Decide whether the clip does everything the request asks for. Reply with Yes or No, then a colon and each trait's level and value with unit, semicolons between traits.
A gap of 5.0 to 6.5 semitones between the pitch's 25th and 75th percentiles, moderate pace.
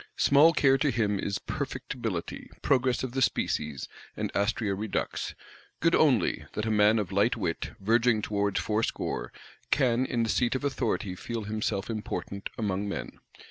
No: average, 3.4 semitones; average, 155 wpm